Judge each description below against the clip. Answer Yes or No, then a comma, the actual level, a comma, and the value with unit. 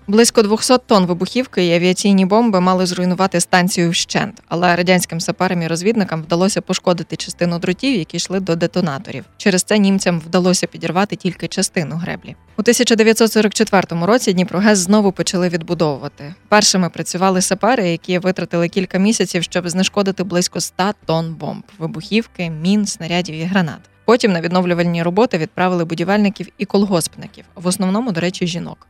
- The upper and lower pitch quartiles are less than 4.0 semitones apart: Yes, average, 2.7 semitones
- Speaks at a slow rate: No, average, 145 wpm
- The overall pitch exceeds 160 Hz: Yes, medium, 185 Hz